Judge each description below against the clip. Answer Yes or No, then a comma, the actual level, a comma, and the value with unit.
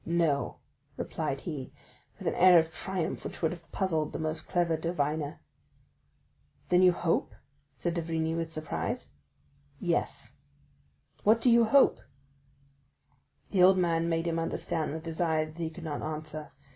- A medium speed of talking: Yes, average, 150 wpm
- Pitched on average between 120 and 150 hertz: No, medium, 165 Hz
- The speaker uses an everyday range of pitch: No, narrow, 2.0 semitones